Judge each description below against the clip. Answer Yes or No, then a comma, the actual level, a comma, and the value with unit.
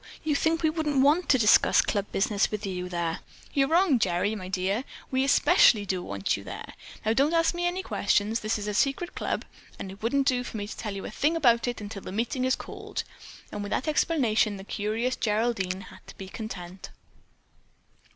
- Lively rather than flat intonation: Yes, wide, 5.8 semitones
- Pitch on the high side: Yes, high, 220 Hz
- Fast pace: Yes, fast, 210 wpm